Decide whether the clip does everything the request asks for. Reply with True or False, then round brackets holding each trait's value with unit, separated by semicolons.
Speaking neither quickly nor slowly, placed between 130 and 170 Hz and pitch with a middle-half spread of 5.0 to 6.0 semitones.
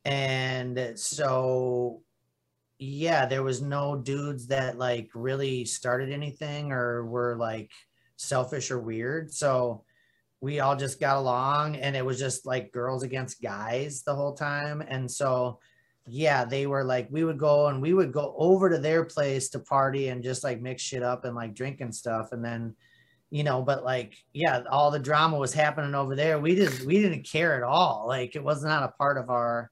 False (190 wpm; 135 Hz; 2.8 semitones)